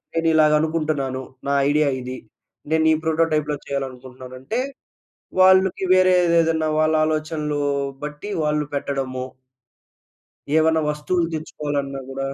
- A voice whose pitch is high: No, medium, 150 Hz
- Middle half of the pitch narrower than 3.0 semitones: Yes, narrow, 2.5 semitones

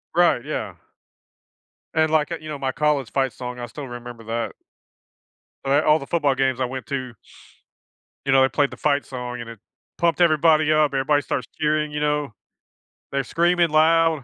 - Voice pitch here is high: No, medium, 145 Hz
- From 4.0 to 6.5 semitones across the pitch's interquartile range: No, average, 3.2 semitones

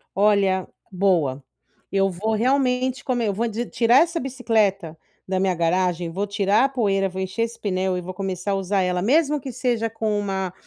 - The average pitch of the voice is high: Yes, high, 200 Hz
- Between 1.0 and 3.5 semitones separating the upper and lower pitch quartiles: No, average, 3.9 semitones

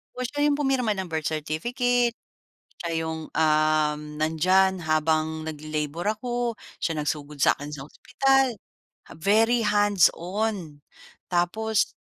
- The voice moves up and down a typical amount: No, wide, 6.4 semitones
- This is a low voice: No, medium, 175 Hz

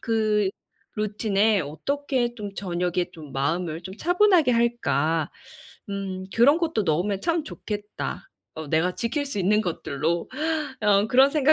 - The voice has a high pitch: Yes, high, 205 Hz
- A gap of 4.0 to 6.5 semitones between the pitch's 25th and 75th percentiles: Yes, wide, 5.5 semitones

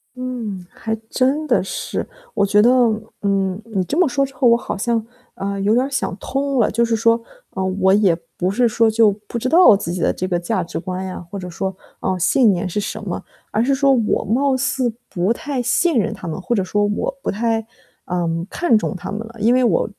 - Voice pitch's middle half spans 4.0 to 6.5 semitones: Yes, average, 4.8 semitones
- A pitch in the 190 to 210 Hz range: No, high, 220 Hz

